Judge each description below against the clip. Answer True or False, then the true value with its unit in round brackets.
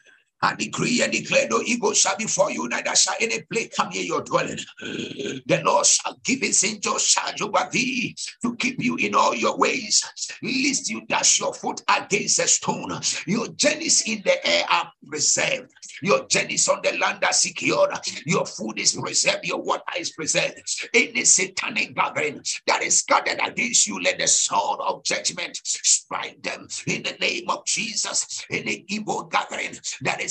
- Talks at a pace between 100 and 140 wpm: False (180 wpm)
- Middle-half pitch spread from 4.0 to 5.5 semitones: True (4.3 semitones)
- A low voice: False (255 Hz)